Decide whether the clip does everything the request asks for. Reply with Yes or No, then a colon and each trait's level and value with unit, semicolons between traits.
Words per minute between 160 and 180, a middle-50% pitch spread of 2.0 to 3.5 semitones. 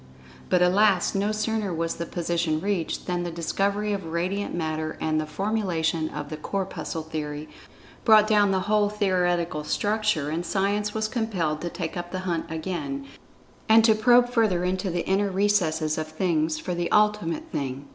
No: average, 170 wpm; average, 4.3 semitones